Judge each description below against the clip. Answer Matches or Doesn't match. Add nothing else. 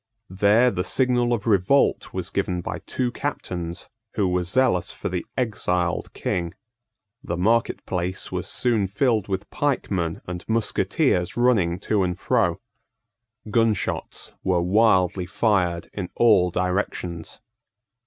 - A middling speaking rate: Doesn't match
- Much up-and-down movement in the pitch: Doesn't match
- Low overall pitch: Matches